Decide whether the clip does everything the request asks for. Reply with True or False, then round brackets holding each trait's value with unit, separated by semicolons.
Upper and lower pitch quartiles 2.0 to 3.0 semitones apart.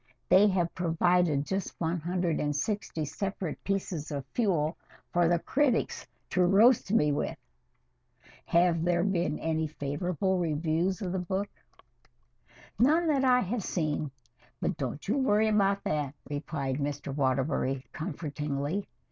False (4.6 semitones)